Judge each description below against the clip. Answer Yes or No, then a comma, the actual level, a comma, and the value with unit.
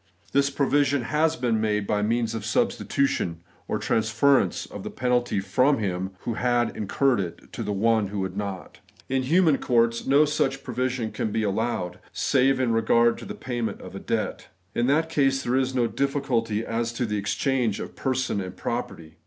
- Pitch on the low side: Yes, low, 120 Hz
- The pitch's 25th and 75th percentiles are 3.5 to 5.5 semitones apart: Yes, average, 4.0 semitones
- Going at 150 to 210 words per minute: Yes, average, 185 wpm